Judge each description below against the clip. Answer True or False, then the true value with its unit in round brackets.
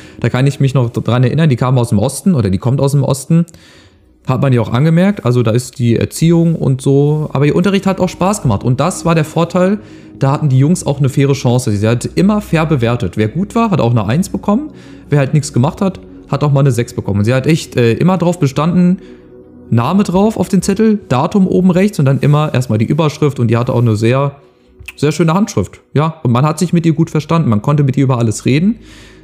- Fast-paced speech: True (250 wpm)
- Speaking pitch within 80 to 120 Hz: False (140 Hz)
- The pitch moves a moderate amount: False (6.0 semitones)